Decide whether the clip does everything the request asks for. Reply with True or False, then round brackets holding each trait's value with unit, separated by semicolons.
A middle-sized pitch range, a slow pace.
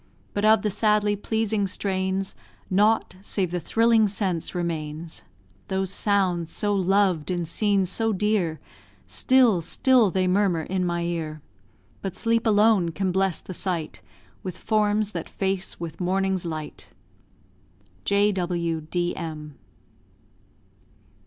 True (3.2 semitones; 120 wpm)